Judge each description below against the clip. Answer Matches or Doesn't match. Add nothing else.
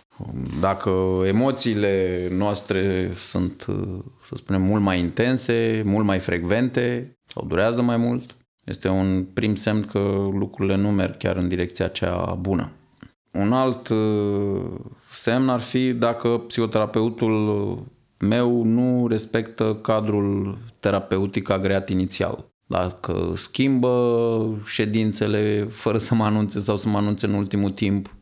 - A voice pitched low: Matches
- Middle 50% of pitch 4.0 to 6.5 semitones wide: Doesn't match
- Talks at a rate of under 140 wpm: Matches